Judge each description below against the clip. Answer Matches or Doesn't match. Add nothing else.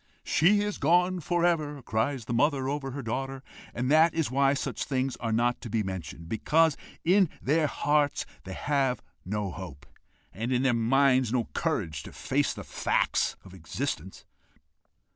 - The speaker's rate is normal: Matches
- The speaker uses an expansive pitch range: Doesn't match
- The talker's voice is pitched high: Doesn't match